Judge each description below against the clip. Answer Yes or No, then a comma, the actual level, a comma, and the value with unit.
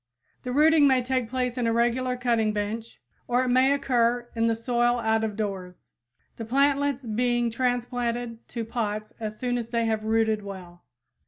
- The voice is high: Yes, high, 235 Hz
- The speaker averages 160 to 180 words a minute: Yes, average, 175 wpm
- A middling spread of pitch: No, narrow, 2.1 semitones